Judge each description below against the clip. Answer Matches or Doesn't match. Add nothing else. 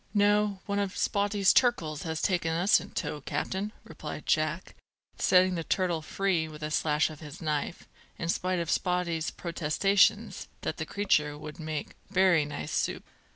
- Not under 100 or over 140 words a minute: Doesn't match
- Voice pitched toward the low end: Doesn't match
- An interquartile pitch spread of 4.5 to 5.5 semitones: Doesn't match